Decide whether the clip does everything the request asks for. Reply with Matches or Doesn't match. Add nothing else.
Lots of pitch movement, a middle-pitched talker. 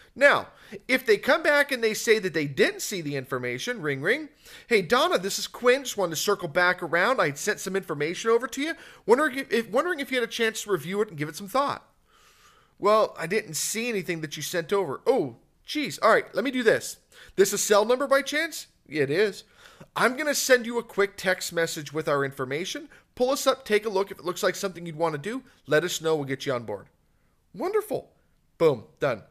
Doesn't match